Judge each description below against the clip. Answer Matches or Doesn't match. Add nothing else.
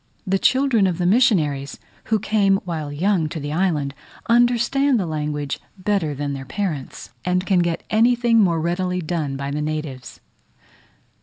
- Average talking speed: Matches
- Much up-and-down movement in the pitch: Matches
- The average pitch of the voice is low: Doesn't match